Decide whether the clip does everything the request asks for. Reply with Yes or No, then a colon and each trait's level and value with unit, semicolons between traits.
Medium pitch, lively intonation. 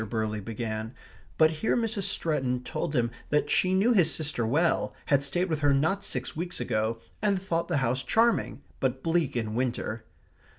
Yes: medium, 145 Hz; wide, 6.4 semitones